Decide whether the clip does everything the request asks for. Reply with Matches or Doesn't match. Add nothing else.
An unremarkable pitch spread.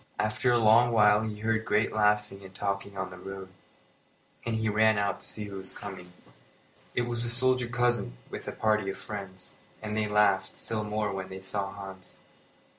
Doesn't match